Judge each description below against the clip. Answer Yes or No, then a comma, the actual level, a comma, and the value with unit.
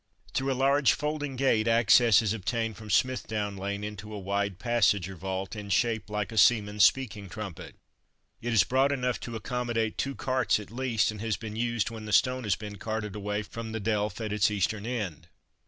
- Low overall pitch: Yes, low, 110 Hz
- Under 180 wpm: No, average, 200 wpm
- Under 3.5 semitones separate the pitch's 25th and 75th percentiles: Yes, average, 2.7 semitones